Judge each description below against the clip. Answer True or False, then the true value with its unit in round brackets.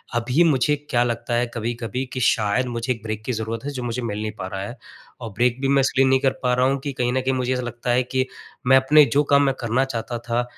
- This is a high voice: False (125 Hz)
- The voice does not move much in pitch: True (2.2 semitones)